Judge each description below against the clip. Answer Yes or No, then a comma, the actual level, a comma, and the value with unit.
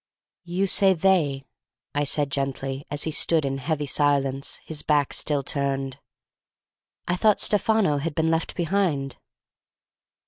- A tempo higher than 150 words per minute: No, slow, 135 wpm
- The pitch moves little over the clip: No, average, 3.8 semitones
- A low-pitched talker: No, medium, 145 Hz